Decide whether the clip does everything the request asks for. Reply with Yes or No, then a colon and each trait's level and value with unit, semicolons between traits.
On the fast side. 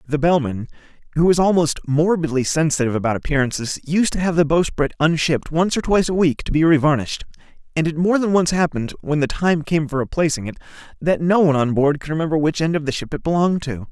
Yes: fast, 220 wpm